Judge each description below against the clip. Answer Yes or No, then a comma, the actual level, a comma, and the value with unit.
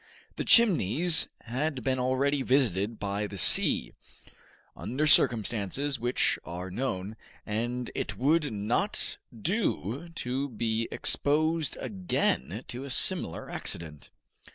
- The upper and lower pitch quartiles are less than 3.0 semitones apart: No, wide, 5.5 semitones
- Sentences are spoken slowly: Yes, slow, 110 wpm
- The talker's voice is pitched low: Yes, low, 125 Hz